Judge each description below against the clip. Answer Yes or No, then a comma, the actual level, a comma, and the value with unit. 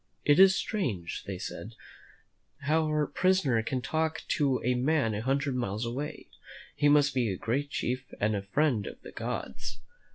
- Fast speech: No, average, 165 wpm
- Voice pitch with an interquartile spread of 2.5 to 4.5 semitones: No, average, 4.9 semitones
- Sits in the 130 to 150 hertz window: Yes, low, 135 Hz